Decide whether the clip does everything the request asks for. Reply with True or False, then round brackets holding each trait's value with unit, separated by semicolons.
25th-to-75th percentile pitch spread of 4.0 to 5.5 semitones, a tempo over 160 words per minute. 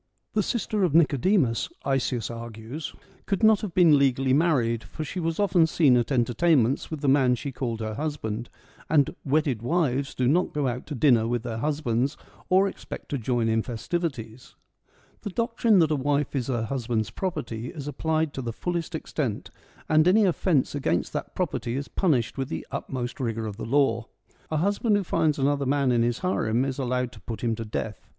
True (5.2 semitones; 195 wpm)